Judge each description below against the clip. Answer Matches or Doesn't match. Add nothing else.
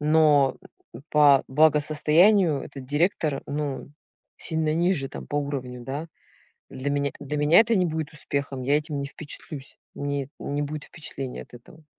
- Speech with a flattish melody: Matches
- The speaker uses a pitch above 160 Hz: Doesn't match